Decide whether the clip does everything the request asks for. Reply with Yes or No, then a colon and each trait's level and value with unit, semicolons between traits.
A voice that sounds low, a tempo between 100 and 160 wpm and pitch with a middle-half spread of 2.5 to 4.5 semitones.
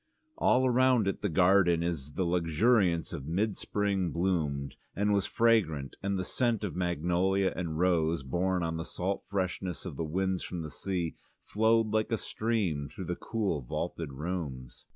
No: very low, 90 Hz; average, 170 wpm; average, 3.8 semitones